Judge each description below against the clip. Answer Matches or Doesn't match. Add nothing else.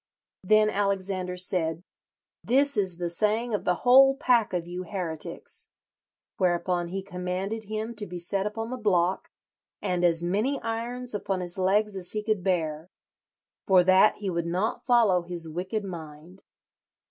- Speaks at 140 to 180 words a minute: Matches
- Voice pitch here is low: Doesn't match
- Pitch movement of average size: Matches